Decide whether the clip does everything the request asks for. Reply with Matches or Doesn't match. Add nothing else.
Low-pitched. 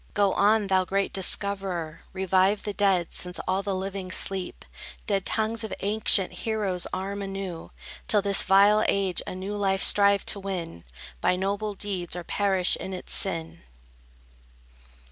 Doesn't match